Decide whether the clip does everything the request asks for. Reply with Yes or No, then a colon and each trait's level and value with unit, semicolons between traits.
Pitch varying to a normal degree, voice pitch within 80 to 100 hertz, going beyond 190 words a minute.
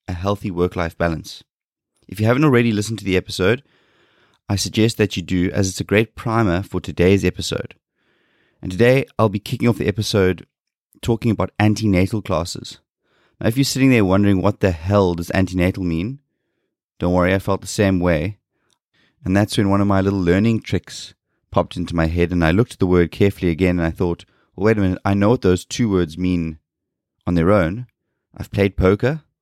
Yes: average, 3.1 semitones; very low, 95 Hz; average, 200 wpm